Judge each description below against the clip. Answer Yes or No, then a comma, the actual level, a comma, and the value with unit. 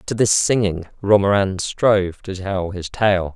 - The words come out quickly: No, average, 160 wpm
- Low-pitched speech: Yes, low, 100 Hz